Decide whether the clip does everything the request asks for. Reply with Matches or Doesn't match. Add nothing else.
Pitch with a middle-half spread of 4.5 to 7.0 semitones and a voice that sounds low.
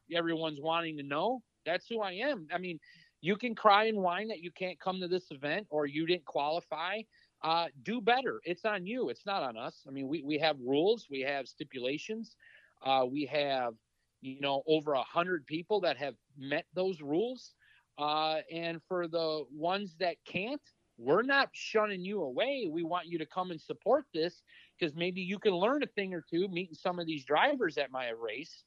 Doesn't match